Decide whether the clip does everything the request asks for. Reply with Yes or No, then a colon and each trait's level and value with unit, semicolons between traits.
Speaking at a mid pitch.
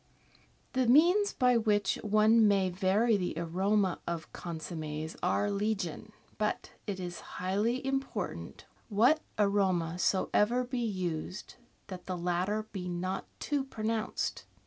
No: high, 200 Hz